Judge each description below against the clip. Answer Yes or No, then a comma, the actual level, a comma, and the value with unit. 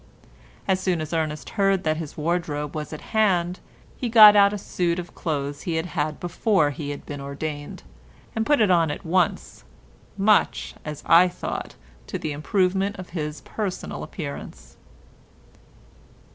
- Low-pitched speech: No, medium, 170 Hz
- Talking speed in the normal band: Yes, average, 160 wpm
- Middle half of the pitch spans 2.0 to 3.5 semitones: No, average, 4.1 semitones